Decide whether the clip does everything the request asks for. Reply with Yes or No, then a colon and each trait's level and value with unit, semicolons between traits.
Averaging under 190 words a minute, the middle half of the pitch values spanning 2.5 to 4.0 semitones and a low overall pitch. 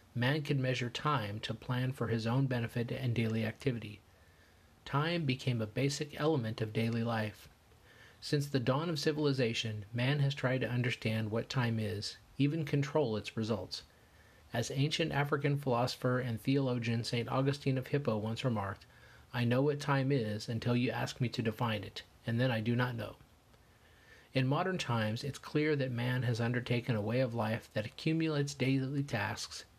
Yes: average, 170 wpm; average, 3.5 semitones; low, 120 Hz